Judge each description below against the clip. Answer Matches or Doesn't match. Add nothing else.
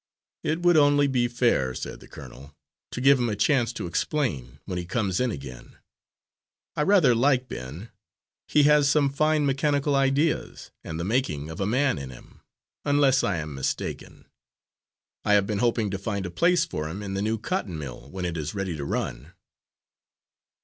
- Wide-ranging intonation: Matches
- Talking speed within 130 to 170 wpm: Doesn't match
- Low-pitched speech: Matches